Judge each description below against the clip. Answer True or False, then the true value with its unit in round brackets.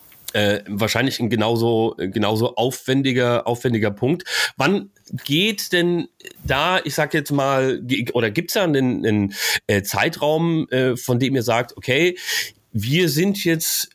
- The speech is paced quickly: False (130 wpm)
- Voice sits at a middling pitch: False (130 Hz)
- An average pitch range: False (6.1 semitones)